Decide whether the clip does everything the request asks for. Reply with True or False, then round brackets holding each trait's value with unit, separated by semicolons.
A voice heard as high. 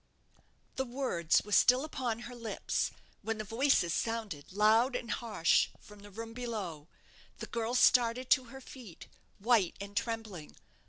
True (225 Hz)